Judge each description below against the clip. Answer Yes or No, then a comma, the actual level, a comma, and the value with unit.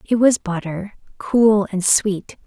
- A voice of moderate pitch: No, high, 200 Hz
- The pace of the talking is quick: No, average, 145 wpm